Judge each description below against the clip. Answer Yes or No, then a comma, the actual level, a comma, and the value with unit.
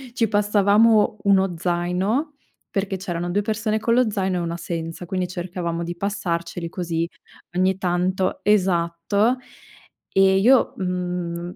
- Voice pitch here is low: No, medium, 185 Hz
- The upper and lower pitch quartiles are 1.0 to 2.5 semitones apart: No, average, 2.9 semitones